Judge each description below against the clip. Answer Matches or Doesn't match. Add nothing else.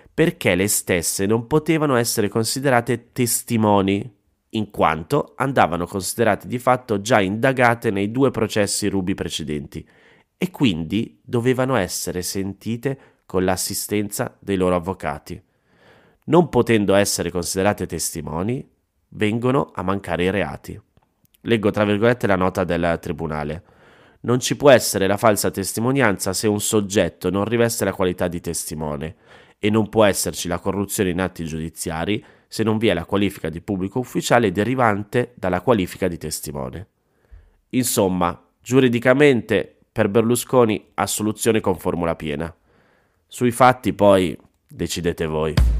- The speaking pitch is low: Matches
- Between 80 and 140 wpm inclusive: Matches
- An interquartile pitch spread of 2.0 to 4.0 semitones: Doesn't match